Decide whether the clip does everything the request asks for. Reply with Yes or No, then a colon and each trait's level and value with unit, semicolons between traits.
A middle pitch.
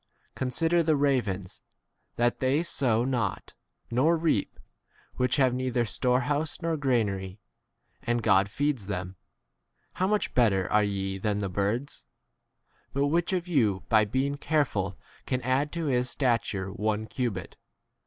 No: low, 125 Hz